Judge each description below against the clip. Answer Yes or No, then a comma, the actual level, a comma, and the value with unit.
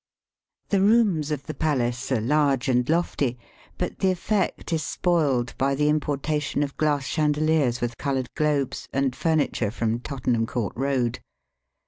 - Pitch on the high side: No, medium, 140 Hz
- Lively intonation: No, average, 3.7 semitones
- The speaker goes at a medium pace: Yes, average, 150 wpm